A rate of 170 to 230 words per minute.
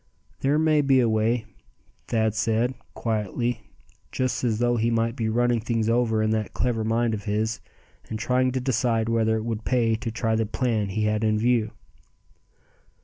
Yes: average, 180 wpm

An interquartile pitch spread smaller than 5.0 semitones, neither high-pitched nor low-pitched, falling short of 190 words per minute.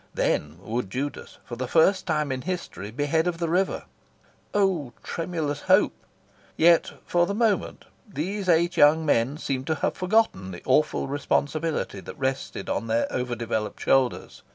No: average, 5.3 semitones; medium, 150 Hz; average, 160 wpm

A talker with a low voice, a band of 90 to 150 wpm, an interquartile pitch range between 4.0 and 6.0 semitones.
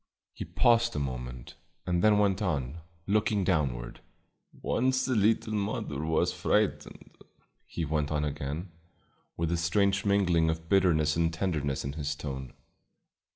Yes: very low, 85 Hz; average, 140 wpm; average, 5.2 semitones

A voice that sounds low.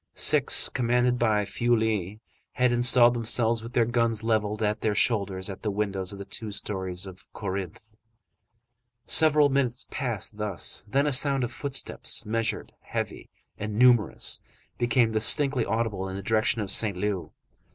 Yes: low, 110 Hz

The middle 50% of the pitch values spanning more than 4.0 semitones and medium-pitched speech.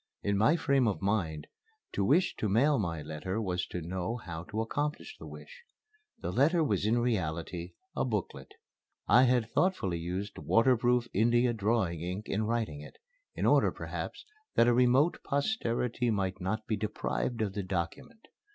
No: average, 4.9 semitones; low, 110 Hz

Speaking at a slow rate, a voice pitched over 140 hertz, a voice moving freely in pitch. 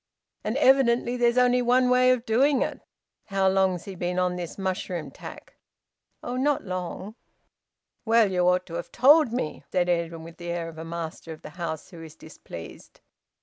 No: average, 185 wpm; high, 190 Hz; wide, 6.1 semitones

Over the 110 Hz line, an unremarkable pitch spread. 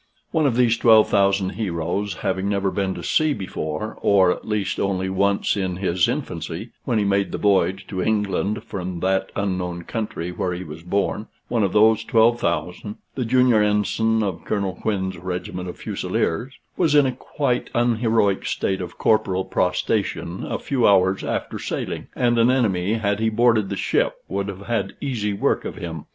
No: low, 100 Hz; average, 3.3 semitones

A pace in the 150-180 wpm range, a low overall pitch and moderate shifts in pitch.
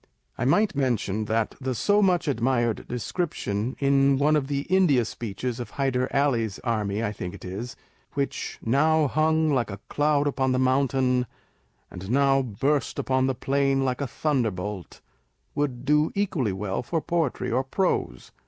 Yes: average, 165 wpm; low, 130 Hz; average, 3.8 semitones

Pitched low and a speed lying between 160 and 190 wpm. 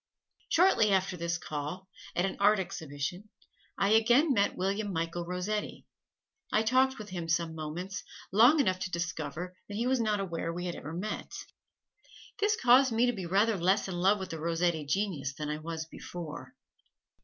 No: medium, 185 Hz; average, 175 wpm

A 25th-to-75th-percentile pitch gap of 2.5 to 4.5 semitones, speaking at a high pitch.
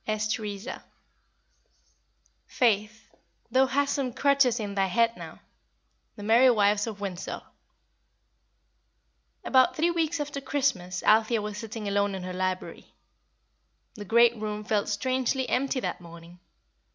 Yes: average, 4.2 semitones; high, 220 Hz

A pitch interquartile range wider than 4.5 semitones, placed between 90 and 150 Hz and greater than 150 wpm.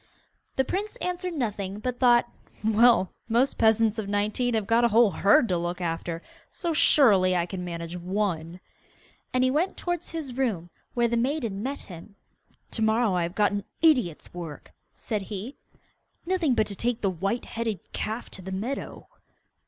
No: average, 5.1 semitones; high, 220 Hz; average, 175 wpm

